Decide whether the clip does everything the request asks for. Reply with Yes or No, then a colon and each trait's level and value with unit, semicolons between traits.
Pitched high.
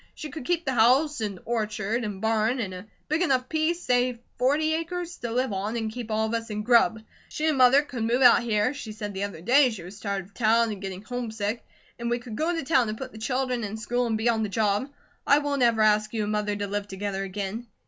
Yes: high, 230 Hz